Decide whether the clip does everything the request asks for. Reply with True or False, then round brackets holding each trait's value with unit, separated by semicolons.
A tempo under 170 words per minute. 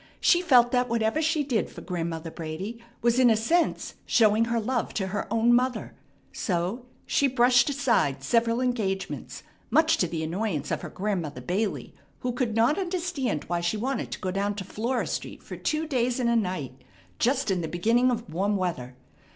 False (185 wpm)